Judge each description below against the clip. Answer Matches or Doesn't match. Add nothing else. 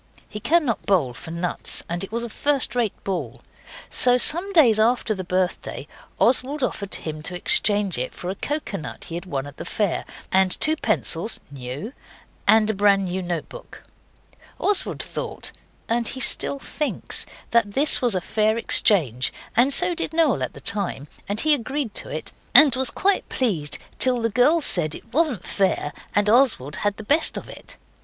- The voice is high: Matches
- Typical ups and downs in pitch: Doesn't match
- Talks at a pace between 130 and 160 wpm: Doesn't match